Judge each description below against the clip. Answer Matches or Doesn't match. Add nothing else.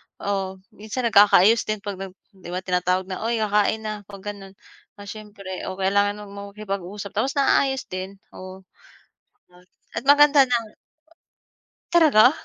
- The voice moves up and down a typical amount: Doesn't match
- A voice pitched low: Doesn't match